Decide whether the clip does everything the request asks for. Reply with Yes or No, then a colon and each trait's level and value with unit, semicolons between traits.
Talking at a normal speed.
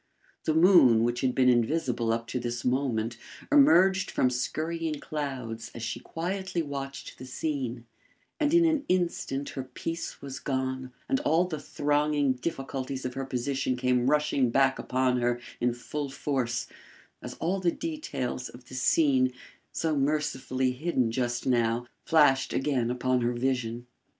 Yes: average, 150 wpm